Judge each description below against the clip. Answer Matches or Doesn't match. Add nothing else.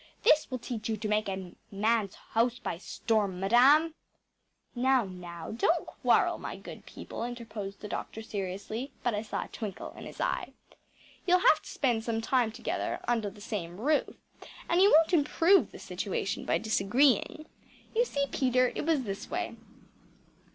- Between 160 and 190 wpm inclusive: Matches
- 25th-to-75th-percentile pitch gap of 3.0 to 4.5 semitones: Doesn't match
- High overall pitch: Matches